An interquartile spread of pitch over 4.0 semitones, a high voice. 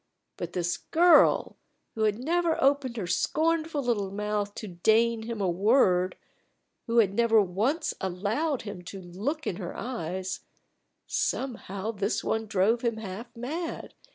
Yes: average, 5.0 semitones; high, 220 Hz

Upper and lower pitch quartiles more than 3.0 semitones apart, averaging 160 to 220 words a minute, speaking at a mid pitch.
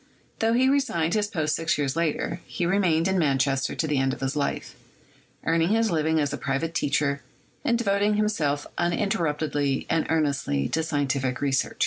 Yes: average, 4.4 semitones; average, 170 wpm; medium, 160 Hz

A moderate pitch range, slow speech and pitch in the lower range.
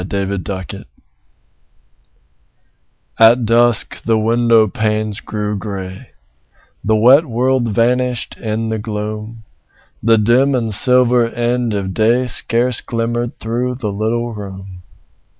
No: narrow, 2.2 semitones; slow, 110 wpm; low, 115 Hz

